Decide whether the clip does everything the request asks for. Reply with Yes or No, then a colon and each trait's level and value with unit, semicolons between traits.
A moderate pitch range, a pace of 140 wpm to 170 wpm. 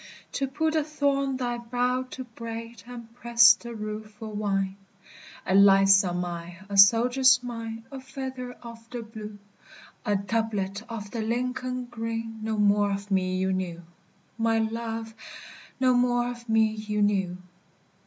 Yes: average, 3.1 semitones; average, 150 wpm